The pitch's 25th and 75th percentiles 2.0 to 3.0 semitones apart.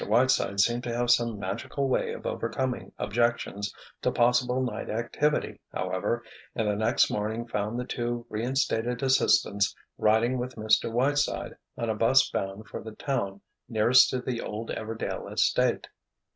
Yes: narrow, 2.5 semitones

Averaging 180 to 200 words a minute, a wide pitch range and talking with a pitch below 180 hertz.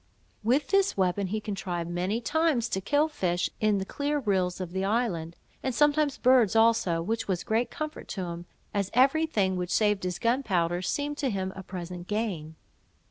No: average, 190 wpm; wide, 6.0 semitones; high, 205 Hz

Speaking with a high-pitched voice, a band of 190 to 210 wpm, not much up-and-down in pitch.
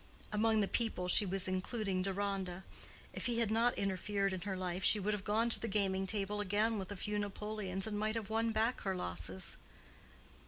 Yes: high, 205 Hz; average, 200 wpm; narrow, 2.3 semitones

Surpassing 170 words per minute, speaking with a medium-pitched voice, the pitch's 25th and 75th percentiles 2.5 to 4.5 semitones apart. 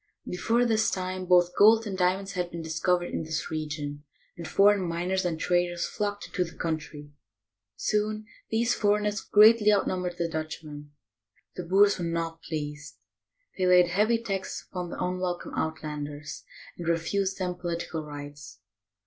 No: average, 155 wpm; medium, 180 Hz; average, 3.7 semitones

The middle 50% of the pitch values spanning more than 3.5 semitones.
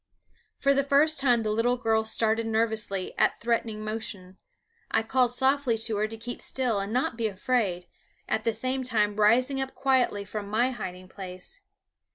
No: average, 3.1 semitones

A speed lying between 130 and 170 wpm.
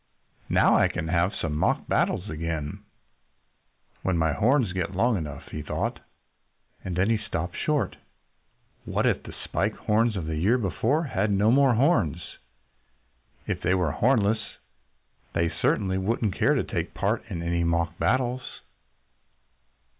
Yes: average, 145 wpm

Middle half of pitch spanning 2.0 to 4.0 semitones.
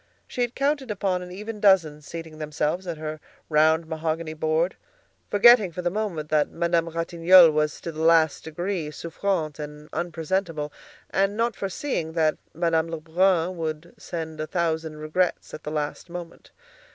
Yes: average, 2.9 semitones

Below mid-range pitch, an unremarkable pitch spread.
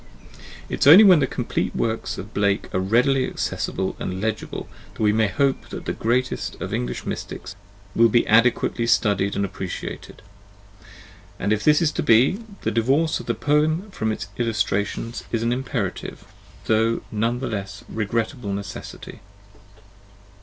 Yes: low, 115 Hz; average, 4.0 semitones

